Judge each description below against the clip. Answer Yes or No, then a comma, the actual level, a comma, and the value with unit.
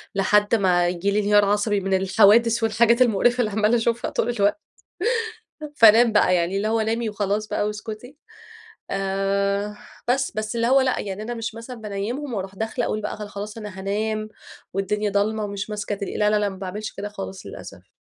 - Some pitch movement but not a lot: No, narrow, 2.2 semitones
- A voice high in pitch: Yes, high, 210 Hz